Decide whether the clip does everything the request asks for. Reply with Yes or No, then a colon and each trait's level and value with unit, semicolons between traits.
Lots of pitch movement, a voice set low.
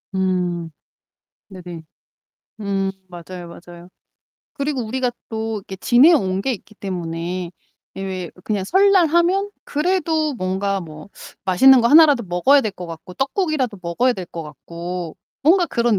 No: wide, 7.1 semitones; high, 195 Hz